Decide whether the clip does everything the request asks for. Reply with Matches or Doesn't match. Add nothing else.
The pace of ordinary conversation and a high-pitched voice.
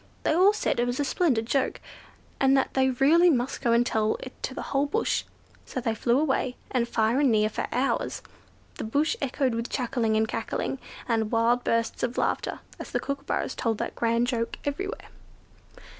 Matches